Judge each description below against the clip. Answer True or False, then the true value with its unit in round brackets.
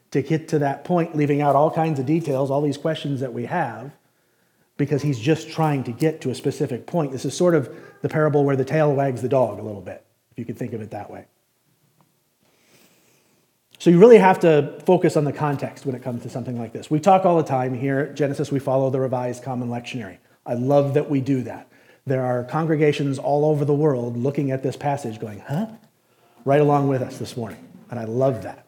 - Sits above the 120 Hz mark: True (140 Hz)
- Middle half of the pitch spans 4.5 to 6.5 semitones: False (3.3 semitones)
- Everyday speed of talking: False (230 wpm)